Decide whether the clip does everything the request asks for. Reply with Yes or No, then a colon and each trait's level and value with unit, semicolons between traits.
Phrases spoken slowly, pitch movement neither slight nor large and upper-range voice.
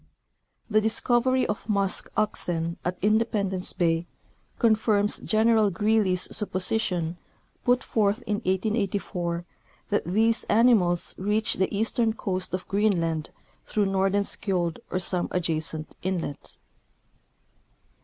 Yes: slow, 105 wpm; average, 3.4 semitones; high, 200 Hz